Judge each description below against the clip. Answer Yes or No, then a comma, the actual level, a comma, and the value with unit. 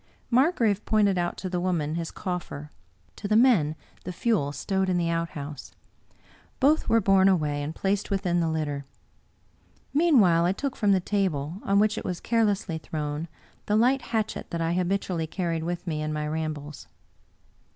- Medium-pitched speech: Yes, medium, 180 Hz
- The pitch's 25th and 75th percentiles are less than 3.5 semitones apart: No, average, 4.5 semitones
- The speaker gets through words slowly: No, average, 170 wpm